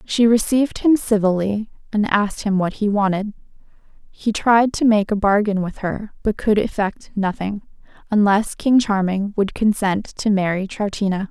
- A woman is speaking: Yes, female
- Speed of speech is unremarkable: Yes, average, 160 wpm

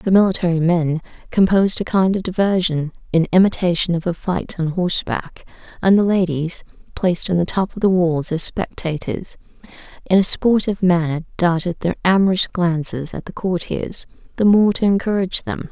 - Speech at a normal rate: Yes, average, 165 wpm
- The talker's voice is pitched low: No, medium, 180 Hz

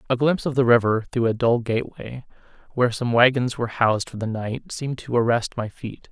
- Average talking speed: No, fast, 215 wpm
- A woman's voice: No, male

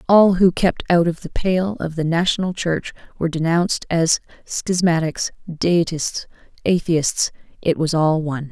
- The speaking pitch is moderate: Yes, medium, 170 Hz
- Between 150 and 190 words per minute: No, average, 140 wpm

